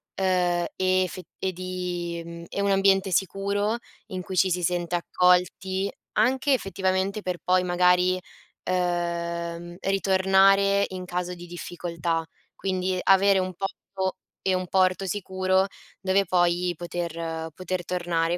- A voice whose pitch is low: No, medium, 185 Hz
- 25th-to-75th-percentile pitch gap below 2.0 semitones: Yes, narrow, 1.6 semitones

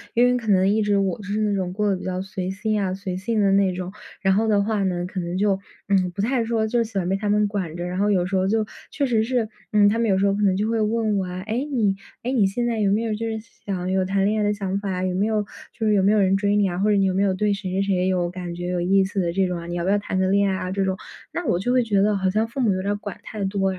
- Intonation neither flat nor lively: No, narrow, 2.3 semitones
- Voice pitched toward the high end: Yes, high, 200 Hz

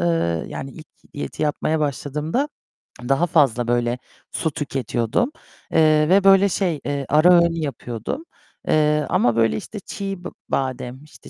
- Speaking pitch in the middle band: Yes, medium, 150 Hz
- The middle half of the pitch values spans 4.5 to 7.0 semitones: Yes, wide, 5.5 semitones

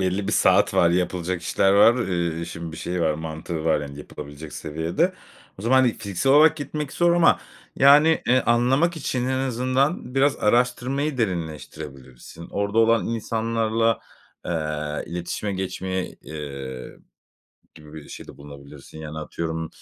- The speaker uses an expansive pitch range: Yes, wide, 7.8 semitones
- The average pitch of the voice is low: Yes, very low, 95 Hz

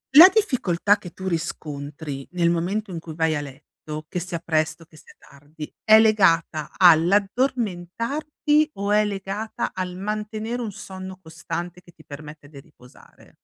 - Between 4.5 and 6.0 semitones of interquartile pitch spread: Yes, average, 5.0 semitones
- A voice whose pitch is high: No, medium, 180 Hz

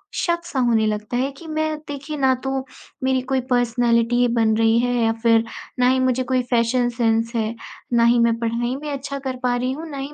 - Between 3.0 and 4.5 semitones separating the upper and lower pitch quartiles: No, narrow, 2.5 semitones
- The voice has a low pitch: No, high, 245 Hz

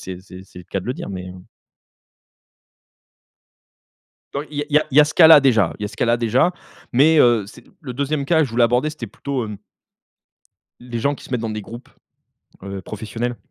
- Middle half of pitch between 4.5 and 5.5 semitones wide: Yes, average, 5.0 semitones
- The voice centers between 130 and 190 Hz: No, low, 120 Hz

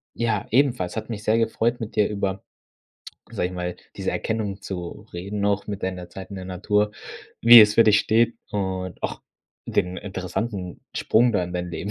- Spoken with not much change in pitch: No, average, 3.2 semitones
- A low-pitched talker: Yes, low, 100 Hz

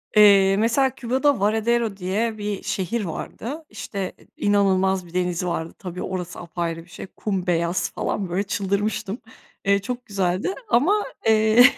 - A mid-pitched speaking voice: No, high, 200 Hz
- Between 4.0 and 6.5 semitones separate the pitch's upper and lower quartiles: No, average, 3.5 semitones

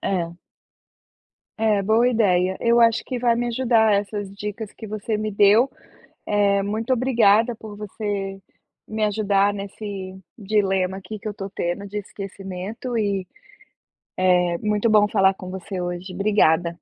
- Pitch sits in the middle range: No, high, 205 Hz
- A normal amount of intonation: No, narrow, 2.1 semitones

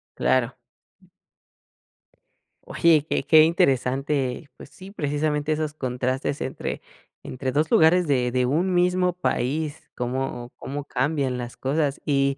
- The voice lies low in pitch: No, medium, 145 Hz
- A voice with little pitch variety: No, average, 3.4 semitones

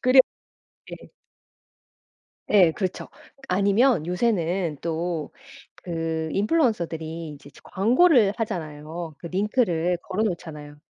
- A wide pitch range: No, average, 4.6 semitones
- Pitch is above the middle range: No, medium, 175 Hz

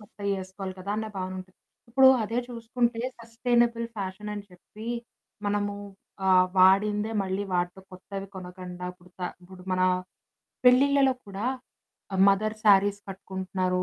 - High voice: Yes, high, 200 Hz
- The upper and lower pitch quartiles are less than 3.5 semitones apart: Yes, average, 3.0 semitones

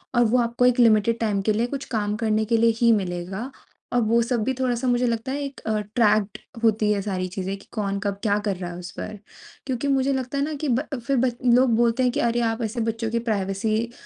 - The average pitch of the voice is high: Yes, high, 230 Hz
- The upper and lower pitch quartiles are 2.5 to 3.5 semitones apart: Yes, average, 2.9 semitones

